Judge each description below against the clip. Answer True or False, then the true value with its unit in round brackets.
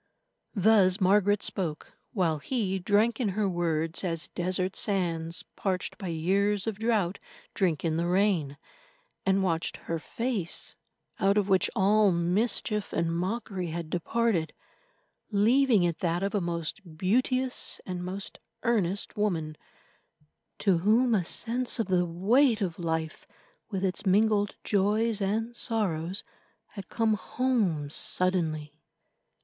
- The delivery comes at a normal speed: False (130 wpm)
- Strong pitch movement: False (3.9 semitones)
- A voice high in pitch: True (195 Hz)